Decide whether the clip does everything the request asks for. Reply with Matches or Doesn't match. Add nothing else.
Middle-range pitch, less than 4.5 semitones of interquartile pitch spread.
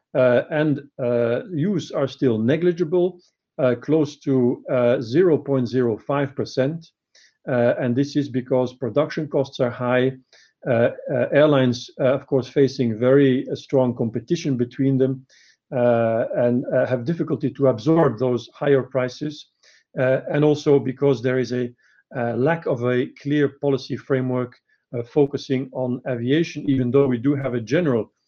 Doesn't match